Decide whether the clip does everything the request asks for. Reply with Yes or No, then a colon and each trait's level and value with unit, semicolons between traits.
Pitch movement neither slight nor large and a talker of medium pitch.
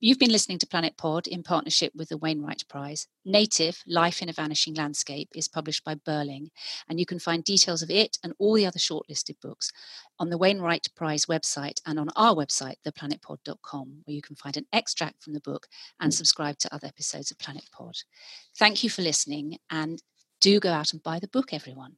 Yes: average, 3.0 semitones; medium, 160 Hz